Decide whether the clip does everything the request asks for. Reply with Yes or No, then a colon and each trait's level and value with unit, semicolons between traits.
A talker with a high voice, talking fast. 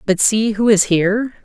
Yes: high, 210 Hz; fast, 210 wpm